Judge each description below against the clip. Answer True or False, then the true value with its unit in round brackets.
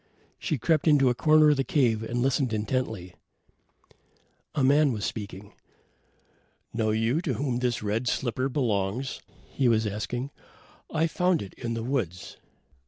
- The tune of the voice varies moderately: True (4.0 semitones)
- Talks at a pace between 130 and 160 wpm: True (155 wpm)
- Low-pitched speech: True (125 Hz)